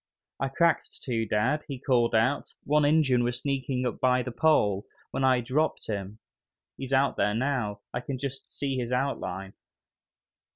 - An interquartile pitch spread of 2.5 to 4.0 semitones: Yes, average, 2.9 semitones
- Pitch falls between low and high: No, low, 130 Hz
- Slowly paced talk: No, average, 165 wpm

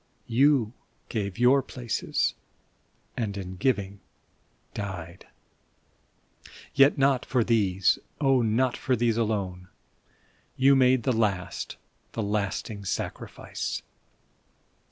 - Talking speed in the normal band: No, slow, 95 wpm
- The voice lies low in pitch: Yes, low, 115 Hz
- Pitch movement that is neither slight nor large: Yes, average, 4.4 semitones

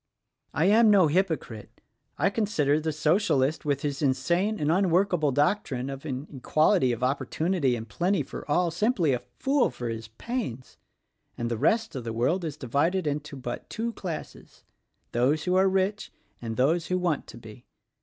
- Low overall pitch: No, medium, 155 Hz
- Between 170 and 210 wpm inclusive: Yes, average, 175 wpm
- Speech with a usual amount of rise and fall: No, wide, 6.2 semitones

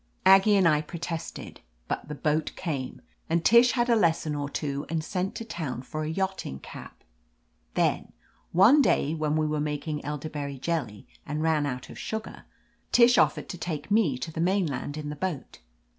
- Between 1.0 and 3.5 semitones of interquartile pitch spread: No, average, 4.2 semitones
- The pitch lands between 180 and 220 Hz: No, medium, 155 Hz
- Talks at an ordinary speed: Yes, average, 180 wpm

